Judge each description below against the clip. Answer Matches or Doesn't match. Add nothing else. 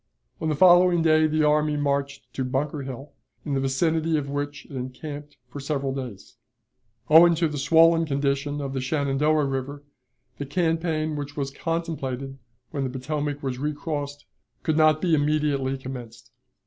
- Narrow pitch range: Matches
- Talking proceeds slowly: Doesn't match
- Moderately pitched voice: Matches